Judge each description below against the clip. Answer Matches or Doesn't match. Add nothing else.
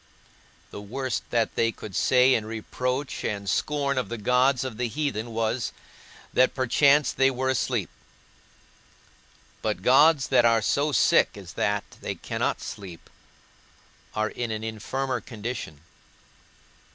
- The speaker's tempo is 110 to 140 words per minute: Matches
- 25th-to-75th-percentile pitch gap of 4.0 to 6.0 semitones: Doesn't match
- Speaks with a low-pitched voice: Matches